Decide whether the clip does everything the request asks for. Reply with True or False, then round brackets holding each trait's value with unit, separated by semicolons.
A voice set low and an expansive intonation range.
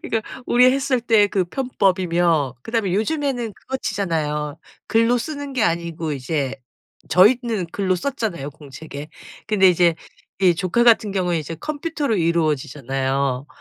False (185 Hz; 7.0 semitones)